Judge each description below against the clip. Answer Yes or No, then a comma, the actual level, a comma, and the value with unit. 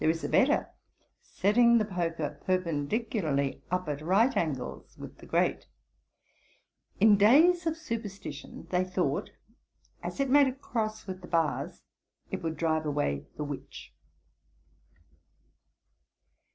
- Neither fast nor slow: No, slow, 125 wpm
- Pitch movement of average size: No, wide, 6.7 semitones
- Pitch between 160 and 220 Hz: Yes, medium, 185 Hz